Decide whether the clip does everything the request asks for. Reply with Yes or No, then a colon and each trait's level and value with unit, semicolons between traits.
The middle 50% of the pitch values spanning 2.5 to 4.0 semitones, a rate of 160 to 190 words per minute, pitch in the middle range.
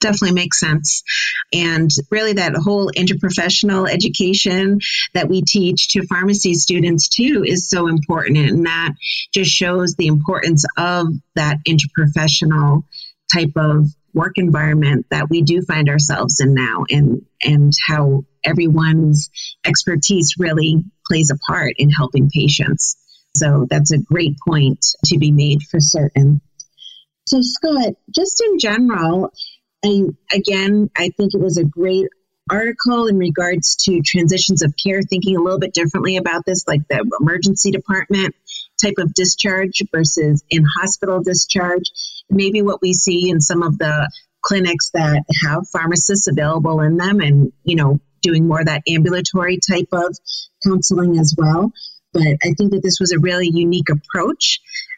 No: average, 3.7 semitones; average, 150 wpm; medium, 170 Hz